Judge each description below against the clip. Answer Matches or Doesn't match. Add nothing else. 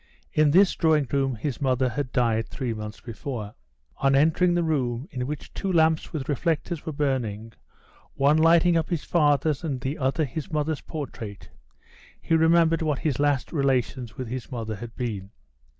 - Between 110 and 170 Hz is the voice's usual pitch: Matches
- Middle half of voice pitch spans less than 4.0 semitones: Doesn't match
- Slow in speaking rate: Doesn't match